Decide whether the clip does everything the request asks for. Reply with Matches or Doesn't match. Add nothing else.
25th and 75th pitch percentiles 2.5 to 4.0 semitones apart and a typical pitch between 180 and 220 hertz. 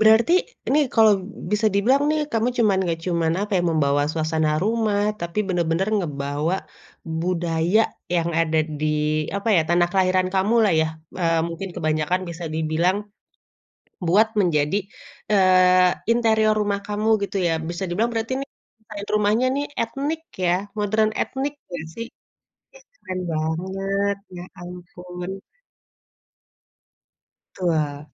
Doesn't match